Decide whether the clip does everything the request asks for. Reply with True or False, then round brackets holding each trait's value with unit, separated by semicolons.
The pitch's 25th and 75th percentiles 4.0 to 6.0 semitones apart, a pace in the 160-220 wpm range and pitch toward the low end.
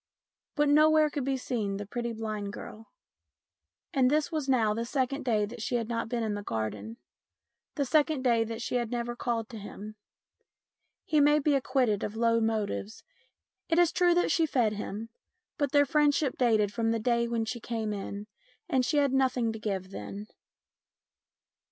False (4.3 semitones; 180 wpm; 235 Hz)